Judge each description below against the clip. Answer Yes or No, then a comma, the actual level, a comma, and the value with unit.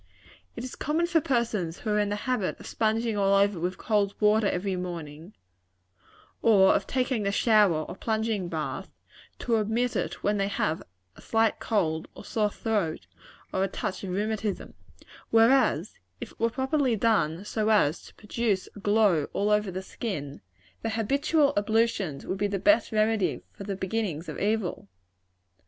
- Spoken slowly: No, average, 170 wpm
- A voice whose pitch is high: Yes, high, 210 Hz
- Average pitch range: Yes, average, 3.1 semitones